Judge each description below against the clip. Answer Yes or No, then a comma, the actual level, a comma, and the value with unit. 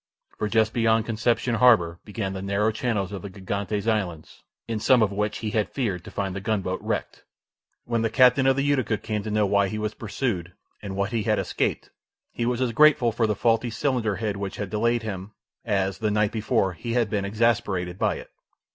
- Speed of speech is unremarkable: No, fast, 210 wpm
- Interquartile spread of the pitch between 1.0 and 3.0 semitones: Yes, average, 2.7 semitones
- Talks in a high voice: No, low, 110 Hz